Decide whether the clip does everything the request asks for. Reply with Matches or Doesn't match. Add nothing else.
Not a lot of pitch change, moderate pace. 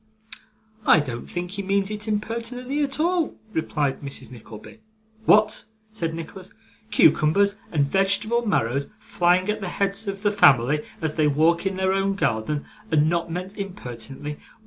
Doesn't match